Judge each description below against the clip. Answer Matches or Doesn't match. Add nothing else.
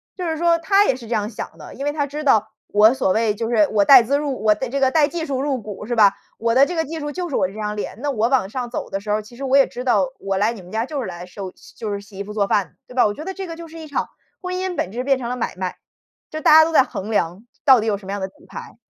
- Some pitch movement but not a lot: Doesn't match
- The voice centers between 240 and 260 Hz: Matches